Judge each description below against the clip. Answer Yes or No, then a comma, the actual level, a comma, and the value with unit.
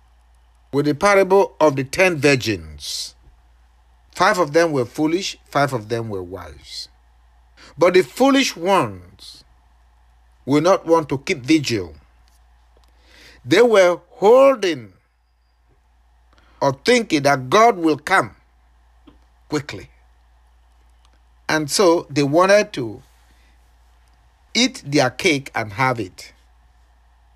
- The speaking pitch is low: Yes, very low, 85 Hz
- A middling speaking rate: No, slow, 105 wpm